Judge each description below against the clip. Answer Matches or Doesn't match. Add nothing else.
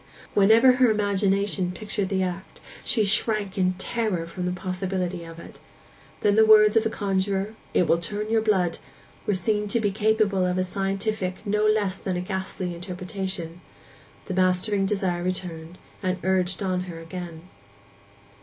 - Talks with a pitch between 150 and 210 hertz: Matches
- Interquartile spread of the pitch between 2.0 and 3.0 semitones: Matches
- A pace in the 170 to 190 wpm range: Doesn't match